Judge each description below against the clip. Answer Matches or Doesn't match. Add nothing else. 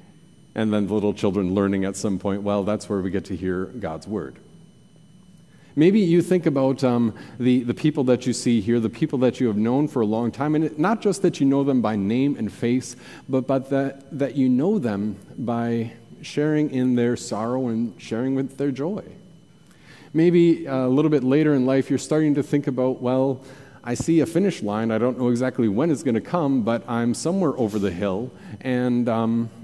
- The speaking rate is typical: Doesn't match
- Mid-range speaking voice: Doesn't match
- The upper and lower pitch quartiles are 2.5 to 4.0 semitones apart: Doesn't match